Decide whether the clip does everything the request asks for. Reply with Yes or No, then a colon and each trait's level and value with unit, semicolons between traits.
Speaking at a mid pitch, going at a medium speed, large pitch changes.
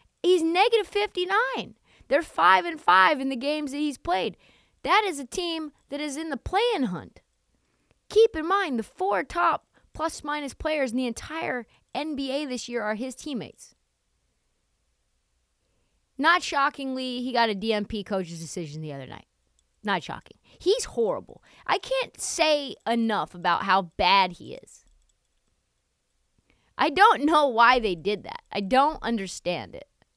No: very high, 280 Hz; average, 150 wpm; wide, 7.3 semitones